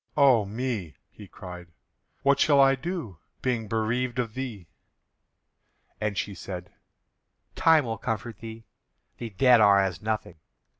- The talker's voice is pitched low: Yes, low, 110 Hz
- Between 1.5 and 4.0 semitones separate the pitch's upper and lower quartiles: No, average, 4.4 semitones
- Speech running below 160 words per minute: Yes, slow, 135 wpm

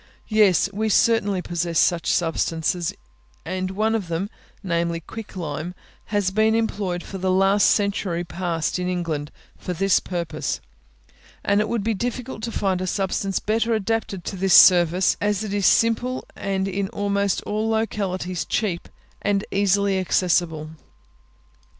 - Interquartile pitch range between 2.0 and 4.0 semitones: Yes, average, 2.9 semitones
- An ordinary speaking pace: Yes, average, 145 wpm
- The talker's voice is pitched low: No, high, 195 Hz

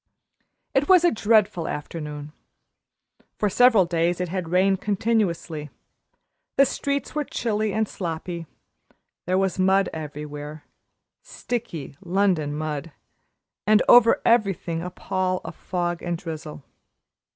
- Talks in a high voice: No, medium, 180 Hz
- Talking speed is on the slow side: Yes, slow, 120 wpm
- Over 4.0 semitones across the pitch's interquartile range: Yes, average, 4.7 semitones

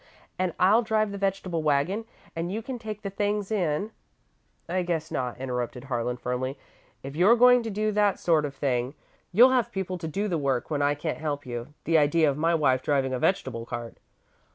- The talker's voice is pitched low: No, medium, 165 Hz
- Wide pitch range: Yes, wide, 6.8 semitones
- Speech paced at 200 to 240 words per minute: Yes, fast, 205 wpm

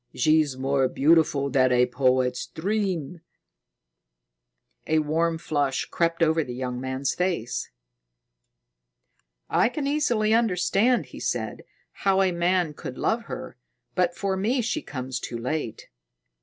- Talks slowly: Yes, slow, 130 wpm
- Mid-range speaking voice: Yes, medium, 160 Hz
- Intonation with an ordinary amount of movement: No, wide, 6.4 semitones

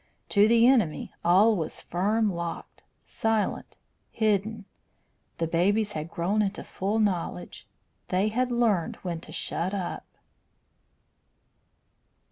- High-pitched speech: Yes, high, 200 Hz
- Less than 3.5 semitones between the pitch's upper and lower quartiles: No, average, 4.0 semitones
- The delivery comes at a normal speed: No, slow, 110 wpm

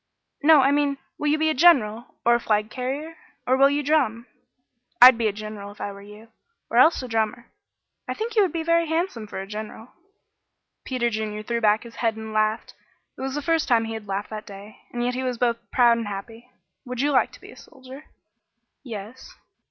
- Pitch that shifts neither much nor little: Yes, average, 4.6 semitones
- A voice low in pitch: No, high, 235 Hz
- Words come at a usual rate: No, fast, 220 wpm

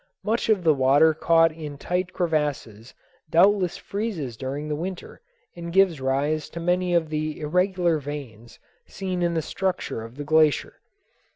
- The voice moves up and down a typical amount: Yes, average, 3.6 semitones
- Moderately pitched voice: Yes, medium, 160 Hz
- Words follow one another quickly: No, average, 155 wpm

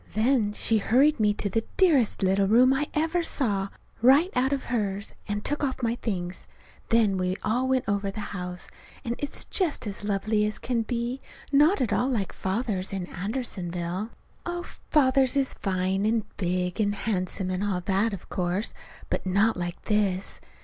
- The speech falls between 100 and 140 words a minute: No, average, 175 wpm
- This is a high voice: Yes, high, 215 Hz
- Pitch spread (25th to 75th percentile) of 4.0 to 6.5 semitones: Yes, average, 4.9 semitones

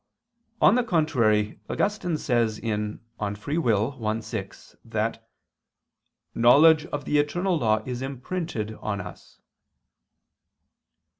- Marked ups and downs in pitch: Yes, wide, 6.6 semitones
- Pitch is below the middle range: Yes, low, 125 Hz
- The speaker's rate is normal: No, slow, 105 wpm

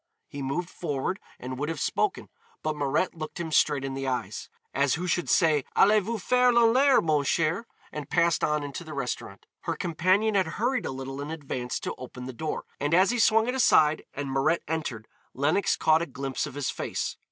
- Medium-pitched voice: Yes, medium, 155 Hz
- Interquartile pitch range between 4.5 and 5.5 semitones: Yes, average, 5.2 semitones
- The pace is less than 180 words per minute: No, fast, 205 wpm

